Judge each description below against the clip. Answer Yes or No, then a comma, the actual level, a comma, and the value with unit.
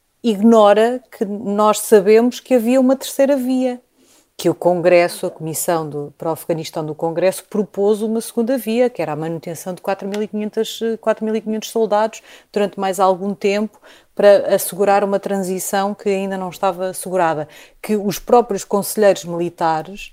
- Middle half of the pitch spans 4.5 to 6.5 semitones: No, average, 3.3 semitones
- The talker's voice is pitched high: Yes, high, 200 Hz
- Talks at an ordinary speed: Yes, average, 145 wpm